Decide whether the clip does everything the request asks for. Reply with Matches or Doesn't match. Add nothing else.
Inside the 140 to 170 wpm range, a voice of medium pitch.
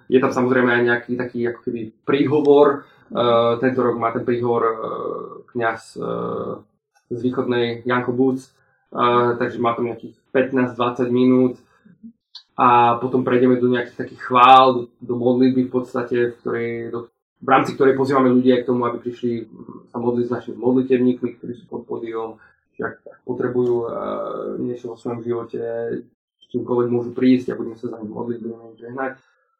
Doesn't match